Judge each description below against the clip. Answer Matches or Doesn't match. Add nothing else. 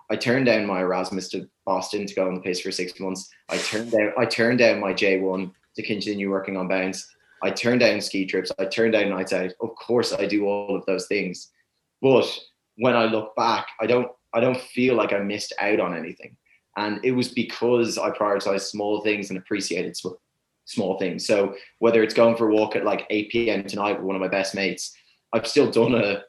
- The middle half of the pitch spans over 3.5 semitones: Doesn't match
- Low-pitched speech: Matches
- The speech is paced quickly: Matches